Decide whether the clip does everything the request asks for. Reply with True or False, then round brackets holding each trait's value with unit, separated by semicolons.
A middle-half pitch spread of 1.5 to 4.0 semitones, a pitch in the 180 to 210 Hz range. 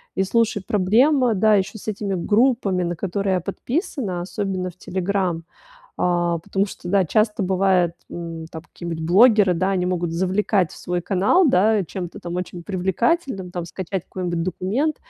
True (2.9 semitones; 190 Hz)